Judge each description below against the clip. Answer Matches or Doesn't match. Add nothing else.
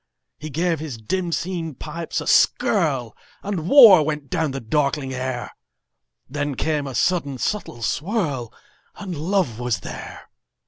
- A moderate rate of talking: Doesn't match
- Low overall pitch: Doesn't match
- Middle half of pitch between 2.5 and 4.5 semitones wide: Doesn't match